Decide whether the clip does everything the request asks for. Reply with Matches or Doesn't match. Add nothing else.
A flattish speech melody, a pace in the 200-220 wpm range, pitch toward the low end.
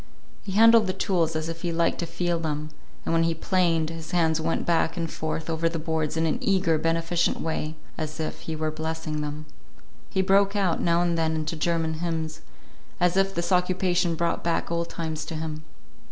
Doesn't match